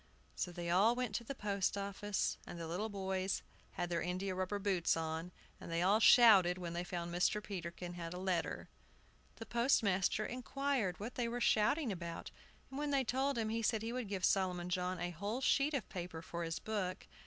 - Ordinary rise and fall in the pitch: Yes, average, 4.3 semitones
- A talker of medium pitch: No, high, 195 Hz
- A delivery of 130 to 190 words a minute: No, average, 200 wpm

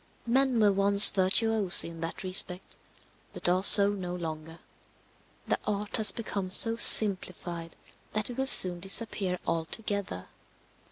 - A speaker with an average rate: No, slow, 130 wpm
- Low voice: No, high, 195 Hz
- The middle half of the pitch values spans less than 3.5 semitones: Yes, average, 3.1 semitones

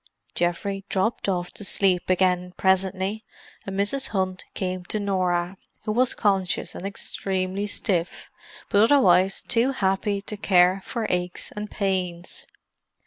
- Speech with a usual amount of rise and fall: No, narrow, 2.0 semitones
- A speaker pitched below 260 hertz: Yes, high, 190 Hz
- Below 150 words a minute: Yes, slow, 135 wpm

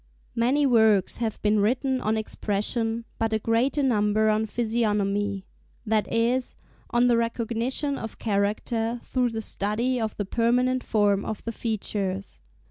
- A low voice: No, high, 225 Hz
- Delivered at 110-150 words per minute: Yes, slow, 135 wpm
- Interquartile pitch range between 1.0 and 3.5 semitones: Yes, narrow, 2.4 semitones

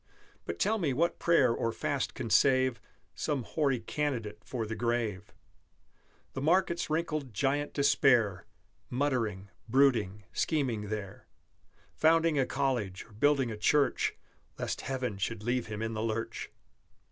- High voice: No, low, 125 Hz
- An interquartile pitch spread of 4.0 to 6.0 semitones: Yes, average, 4.9 semitones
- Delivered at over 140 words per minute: No, slow, 135 wpm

